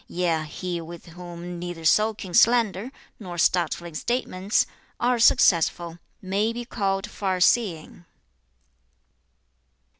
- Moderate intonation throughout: Yes, average, 3.7 semitones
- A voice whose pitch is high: No, medium, 180 Hz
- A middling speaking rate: No, slow, 95 wpm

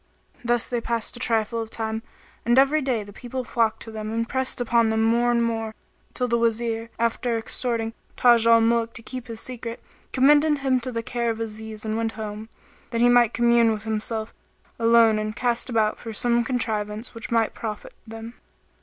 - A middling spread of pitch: No, narrow, 1.4 semitones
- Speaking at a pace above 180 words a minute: Yes, average, 195 wpm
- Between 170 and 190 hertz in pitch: No, high, 230 Hz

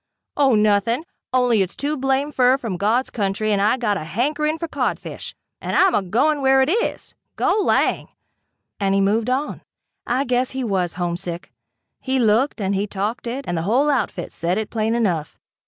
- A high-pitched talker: Yes, high, 230 Hz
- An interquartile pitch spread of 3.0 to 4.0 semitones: No, average, 5.2 semitones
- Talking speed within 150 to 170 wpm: No, average, 185 wpm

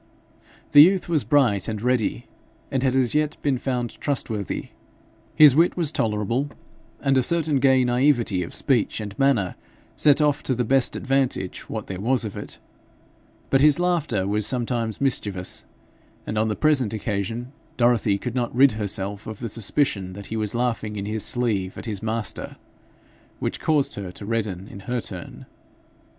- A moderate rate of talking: Yes, average, 170 wpm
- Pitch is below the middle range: Yes, low, 120 Hz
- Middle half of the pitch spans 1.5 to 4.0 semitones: No, average, 4.6 semitones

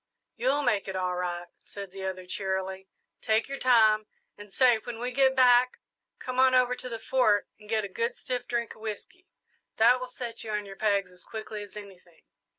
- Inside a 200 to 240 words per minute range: Yes, fast, 205 wpm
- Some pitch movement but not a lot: Yes, average, 4.3 semitones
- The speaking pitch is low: No, high, 220 Hz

